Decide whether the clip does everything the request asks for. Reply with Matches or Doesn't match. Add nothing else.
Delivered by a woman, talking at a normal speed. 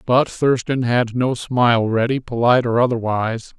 Doesn't match